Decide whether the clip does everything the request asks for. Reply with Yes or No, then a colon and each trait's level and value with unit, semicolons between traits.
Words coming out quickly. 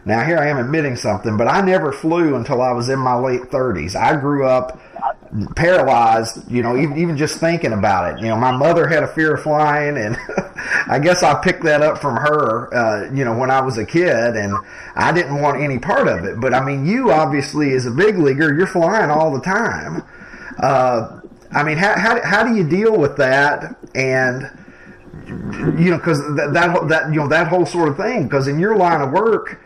Yes: fast, 220 wpm